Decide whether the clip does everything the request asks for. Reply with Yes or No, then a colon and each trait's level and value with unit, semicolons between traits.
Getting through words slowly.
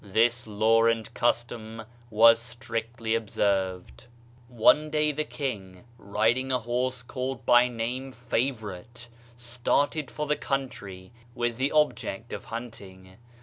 Yes: slow, 120 wpm